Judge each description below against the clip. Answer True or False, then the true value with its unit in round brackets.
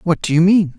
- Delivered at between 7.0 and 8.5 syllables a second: False (5.5 syllables/s)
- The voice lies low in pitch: False (170 Hz)